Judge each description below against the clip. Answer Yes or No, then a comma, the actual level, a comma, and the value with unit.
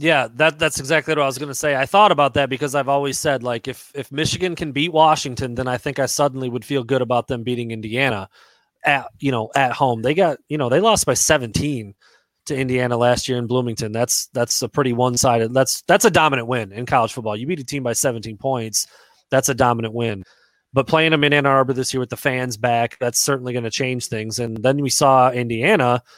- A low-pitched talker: Yes, low, 130 Hz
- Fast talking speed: Yes, fast, 235 wpm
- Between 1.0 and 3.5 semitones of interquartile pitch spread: Yes, average, 2.7 semitones